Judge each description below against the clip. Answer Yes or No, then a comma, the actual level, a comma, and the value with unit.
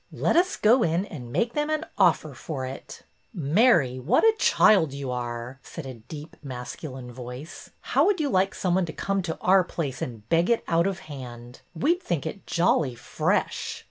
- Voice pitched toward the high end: No, medium, 160 Hz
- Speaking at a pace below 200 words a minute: No, fast, 205 wpm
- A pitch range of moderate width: No, wide, 7.2 semitones